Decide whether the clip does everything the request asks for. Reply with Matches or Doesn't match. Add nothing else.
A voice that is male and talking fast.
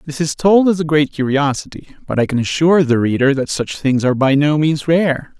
Matches